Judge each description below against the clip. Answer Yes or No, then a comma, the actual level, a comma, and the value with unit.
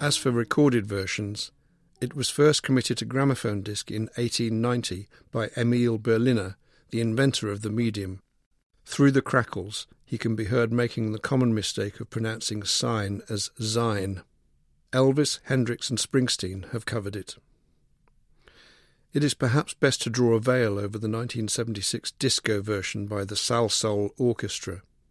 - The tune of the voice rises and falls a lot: No, average, 3.3 semitones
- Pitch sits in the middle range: No, low, 115 Hz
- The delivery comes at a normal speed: Yes, average, 155 wpm